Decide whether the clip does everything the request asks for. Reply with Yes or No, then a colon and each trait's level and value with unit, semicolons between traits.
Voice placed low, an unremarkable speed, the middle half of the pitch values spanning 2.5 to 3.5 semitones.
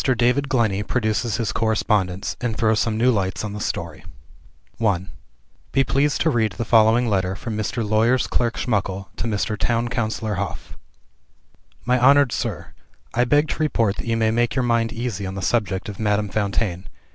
Yes: low, 110 Hz; average, 180 wpm; average, 2.8 semitones